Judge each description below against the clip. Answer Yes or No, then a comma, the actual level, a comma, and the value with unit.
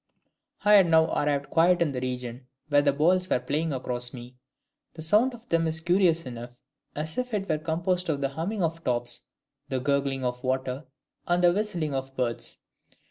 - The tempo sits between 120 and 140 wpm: No, average, 190 wpm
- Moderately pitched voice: Yes, medium, 155 Hz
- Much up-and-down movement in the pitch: No, average, 5.0 semitones